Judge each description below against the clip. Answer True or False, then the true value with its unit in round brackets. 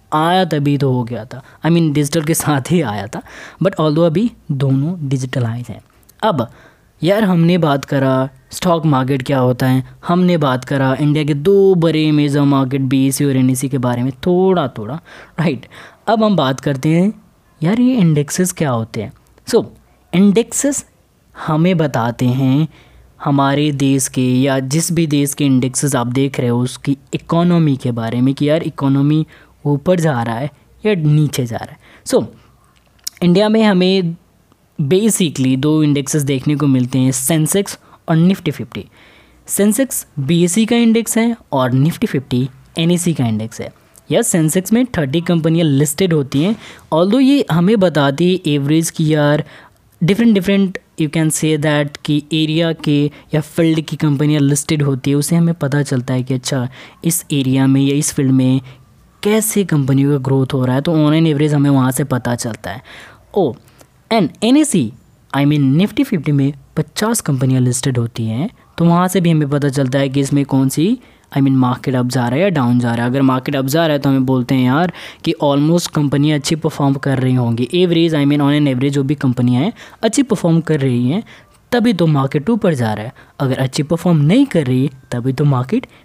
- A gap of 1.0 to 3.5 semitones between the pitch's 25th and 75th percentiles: False (4.1 semitones)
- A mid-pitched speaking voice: True (145 Hz)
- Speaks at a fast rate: True (195 wpm)